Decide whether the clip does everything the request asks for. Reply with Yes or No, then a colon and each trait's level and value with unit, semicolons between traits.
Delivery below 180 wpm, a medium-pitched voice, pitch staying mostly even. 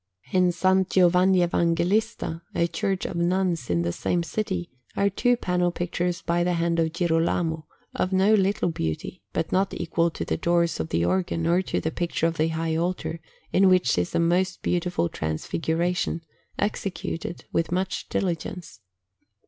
Yes: average, 165 wpm; medium, 175 Hz; narrow, 1.9 semitones